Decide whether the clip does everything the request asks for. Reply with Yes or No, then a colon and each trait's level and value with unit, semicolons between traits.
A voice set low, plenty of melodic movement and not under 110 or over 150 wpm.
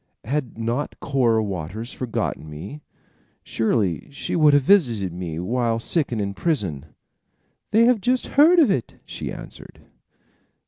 Yes: low, 120 Hz; wide, 7.3 semitones; average, 140 wpm